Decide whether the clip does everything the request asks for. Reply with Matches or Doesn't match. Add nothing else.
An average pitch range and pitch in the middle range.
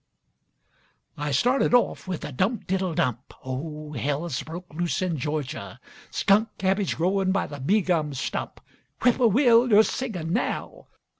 Doesn't match